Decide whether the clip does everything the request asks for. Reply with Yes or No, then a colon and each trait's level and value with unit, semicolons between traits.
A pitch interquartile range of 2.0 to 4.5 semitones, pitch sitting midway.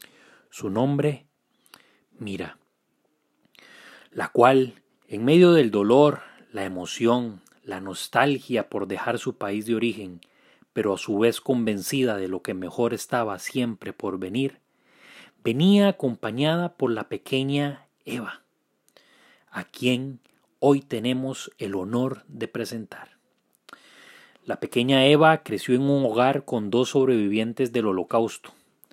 No: average, 3.5 semitones; low, 125 Hz